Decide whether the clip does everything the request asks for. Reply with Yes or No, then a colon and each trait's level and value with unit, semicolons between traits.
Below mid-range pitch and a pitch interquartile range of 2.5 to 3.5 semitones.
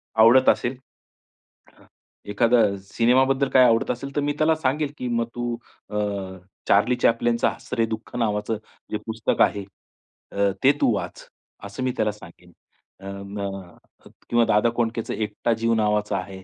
Yes: low, 115 Hz; average, 2.8 semitones